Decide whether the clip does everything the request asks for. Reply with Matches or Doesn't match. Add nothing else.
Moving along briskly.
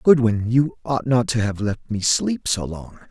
Matches